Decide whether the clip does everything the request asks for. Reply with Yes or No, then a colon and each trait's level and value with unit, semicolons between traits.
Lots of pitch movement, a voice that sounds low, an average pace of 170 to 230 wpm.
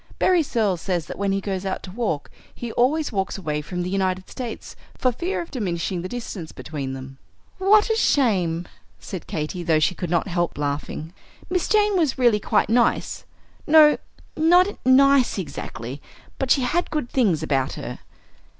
No: wide, 8.1 semitones; high, 195 Hz; average, 175 wpm